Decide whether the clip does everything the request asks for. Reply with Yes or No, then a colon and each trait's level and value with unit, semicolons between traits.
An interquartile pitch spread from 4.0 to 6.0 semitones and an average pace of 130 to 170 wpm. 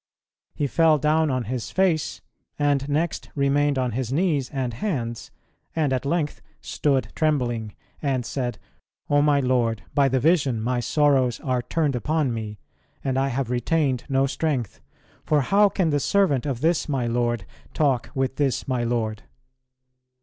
No: average, 3.4 semitones; average, 155 wpm